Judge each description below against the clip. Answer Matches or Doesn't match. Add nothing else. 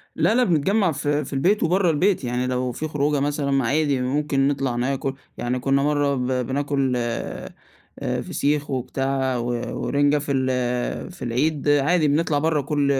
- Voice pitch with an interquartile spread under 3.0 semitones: Matches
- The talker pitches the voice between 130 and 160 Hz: Matches